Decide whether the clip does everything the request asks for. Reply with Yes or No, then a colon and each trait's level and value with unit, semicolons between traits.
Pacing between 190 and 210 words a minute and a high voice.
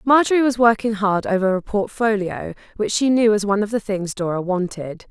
Yes: average, 200 wpm; high, 210 Hz